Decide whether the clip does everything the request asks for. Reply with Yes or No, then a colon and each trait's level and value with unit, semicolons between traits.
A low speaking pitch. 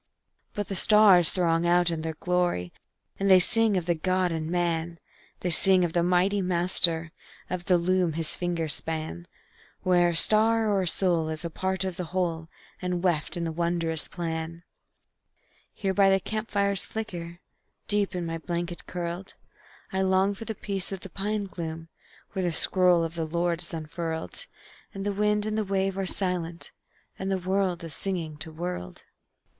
No: medium, 175 Hz